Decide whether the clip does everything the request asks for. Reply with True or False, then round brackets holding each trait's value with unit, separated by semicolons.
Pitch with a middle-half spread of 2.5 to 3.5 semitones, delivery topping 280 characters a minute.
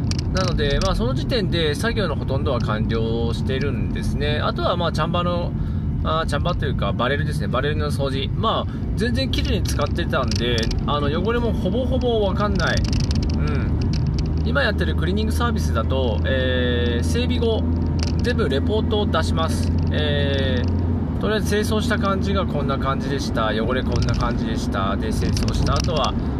True (3.0 semitones; 365 characters per minute)